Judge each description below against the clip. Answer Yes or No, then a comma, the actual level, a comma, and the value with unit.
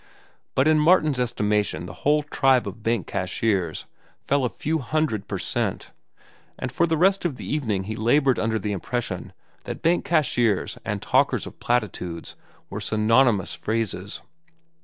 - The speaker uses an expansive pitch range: Yes, wide, 6.1 semitones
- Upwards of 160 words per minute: No, average, 155 wpm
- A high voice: No, low, 120 Hz